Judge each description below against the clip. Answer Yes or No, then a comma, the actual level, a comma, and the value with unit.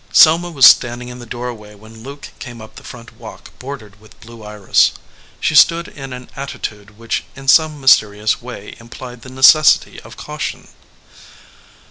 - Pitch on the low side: Yes, low, 120 Hz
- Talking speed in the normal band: Yes, average, 160 wpm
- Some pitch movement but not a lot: Yes, average, 3.7 semitones